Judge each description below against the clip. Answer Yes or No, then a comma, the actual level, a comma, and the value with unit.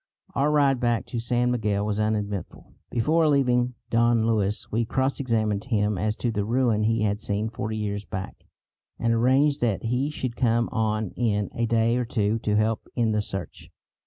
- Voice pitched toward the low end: Yes, low, 115 Hz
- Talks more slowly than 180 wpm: No, average, 185 wpm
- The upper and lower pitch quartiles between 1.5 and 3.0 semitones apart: Yes, narrow, 2.6 semitones